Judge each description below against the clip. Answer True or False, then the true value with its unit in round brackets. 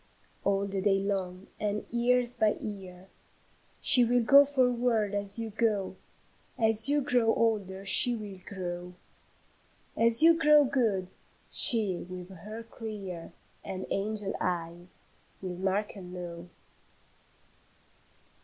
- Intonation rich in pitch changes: False (3.7 semitones)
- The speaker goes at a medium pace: False (120 wpm)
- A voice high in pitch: True (205 Hz)